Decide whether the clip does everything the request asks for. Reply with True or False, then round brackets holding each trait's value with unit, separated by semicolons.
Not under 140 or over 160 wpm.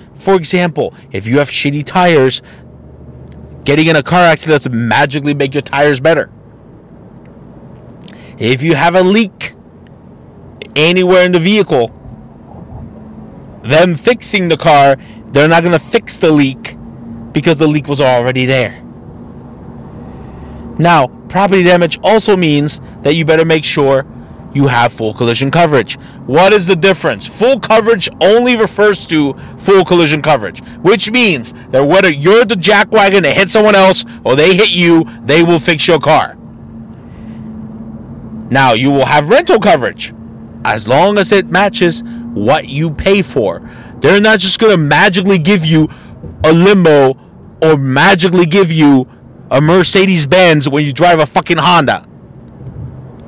True (145 wpm)